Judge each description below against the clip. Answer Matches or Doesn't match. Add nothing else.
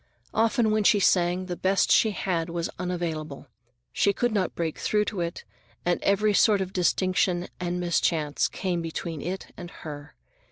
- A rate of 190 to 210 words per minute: Doesn't match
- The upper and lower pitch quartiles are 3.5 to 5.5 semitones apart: Doesn't match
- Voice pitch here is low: Doesn't match